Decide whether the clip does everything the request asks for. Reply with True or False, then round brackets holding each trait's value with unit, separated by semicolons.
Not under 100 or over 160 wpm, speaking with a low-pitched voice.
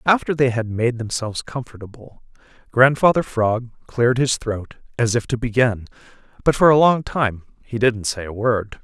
False (170 wpm; 120 Hz)